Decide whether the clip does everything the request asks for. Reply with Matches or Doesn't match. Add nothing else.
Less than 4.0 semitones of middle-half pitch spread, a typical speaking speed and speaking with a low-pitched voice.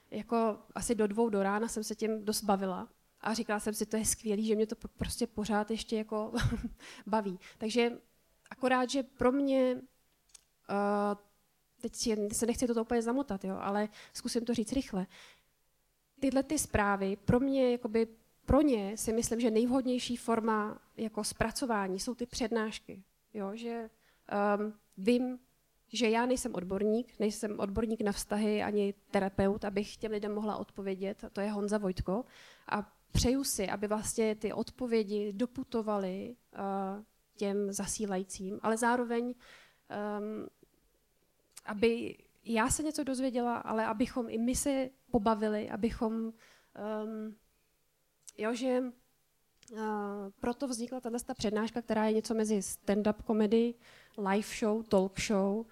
Doesn't match